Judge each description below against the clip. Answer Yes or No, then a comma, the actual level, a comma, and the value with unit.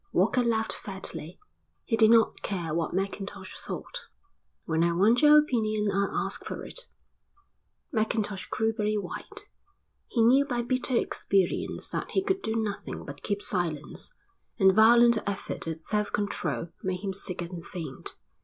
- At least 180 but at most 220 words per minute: No, average, 155 wpm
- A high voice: Yes, high, 210 Hz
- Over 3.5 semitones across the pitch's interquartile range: Yes, average, 4.2 semitones